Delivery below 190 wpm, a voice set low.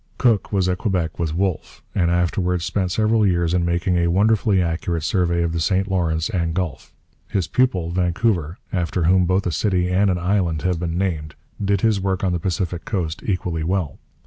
No: average, 195 wpm; very low, 90 Hz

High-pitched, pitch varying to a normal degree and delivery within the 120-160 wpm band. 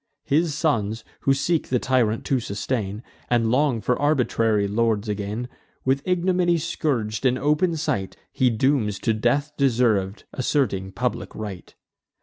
No: low, 125 Hz; average, 5.0 semitones; slow, 135 wpm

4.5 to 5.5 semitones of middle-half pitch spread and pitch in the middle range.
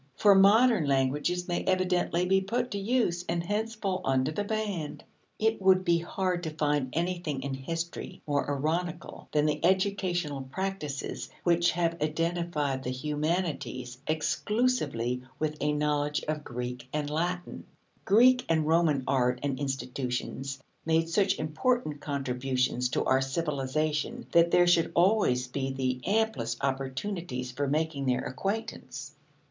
Yes: average, 5.2 semitones; medium, 155 Hz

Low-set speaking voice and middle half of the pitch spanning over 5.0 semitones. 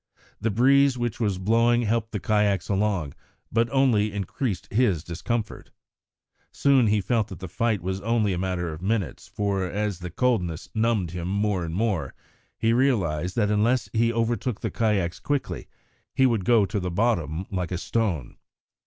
No: low, 105 Hz; average, 4.2 semitones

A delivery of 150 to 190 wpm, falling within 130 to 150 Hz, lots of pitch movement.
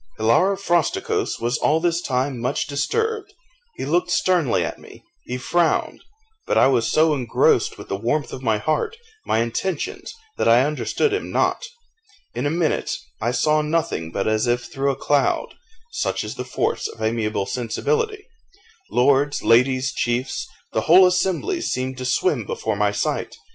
Yes: average, 165 wpm; low, 135 Hz; wide, 6.5 semitones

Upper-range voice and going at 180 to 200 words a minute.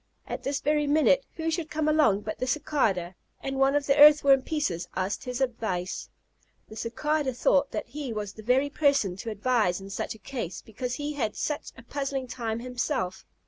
Yes: very high, 260 Hz; average, 195 wpm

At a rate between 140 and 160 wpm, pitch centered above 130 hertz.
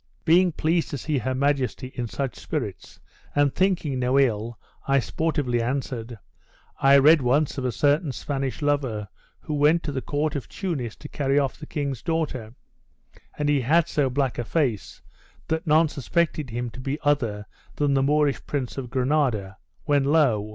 No: average, 170 wpm; medium, 140 Hz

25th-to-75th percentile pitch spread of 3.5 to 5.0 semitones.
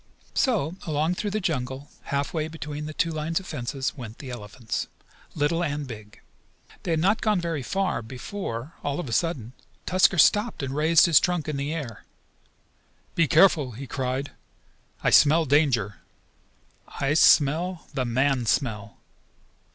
Yes: average, 4.4 semitones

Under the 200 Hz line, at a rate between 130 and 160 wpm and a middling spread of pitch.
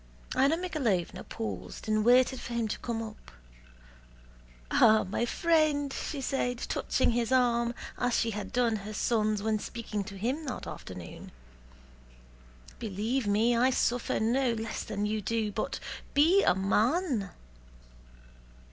No: high, 230 Hz; average, 140 wpm; average, 3.4 semitones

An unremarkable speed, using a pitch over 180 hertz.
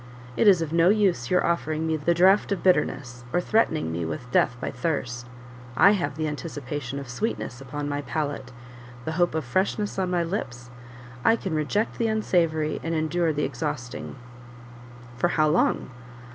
No: average, 175 wpm; medium, 155 Hz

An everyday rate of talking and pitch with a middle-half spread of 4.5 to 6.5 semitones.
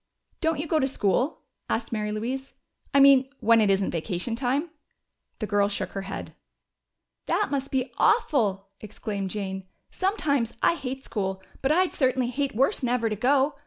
Yes: average, 165 wpm; average, 5.2 semitones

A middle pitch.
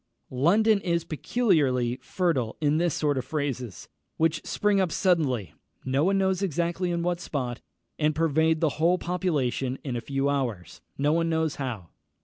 Yes: medium, 155 Hz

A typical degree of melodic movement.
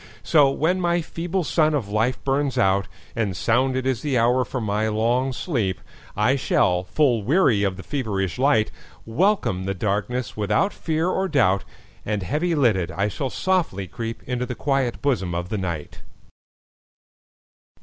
No: wide, 6.0 semitones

